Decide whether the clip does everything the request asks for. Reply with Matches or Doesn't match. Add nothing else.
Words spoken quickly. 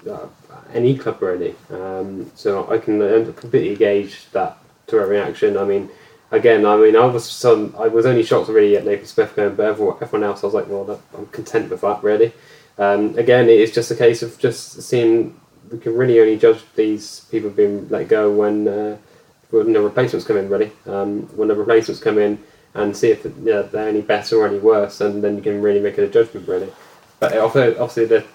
Matches